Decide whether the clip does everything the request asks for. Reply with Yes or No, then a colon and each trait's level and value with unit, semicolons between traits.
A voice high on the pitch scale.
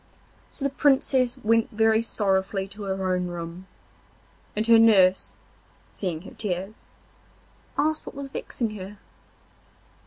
Yes: high, 210 Hz